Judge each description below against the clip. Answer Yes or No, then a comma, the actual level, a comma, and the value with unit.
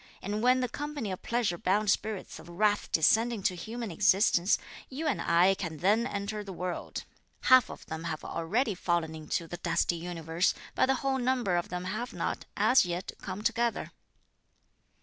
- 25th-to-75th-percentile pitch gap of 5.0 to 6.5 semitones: Yes, average, 5.3 semitones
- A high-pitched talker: Yes, high, 200 Hz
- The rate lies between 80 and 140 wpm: No, average, 175 wpm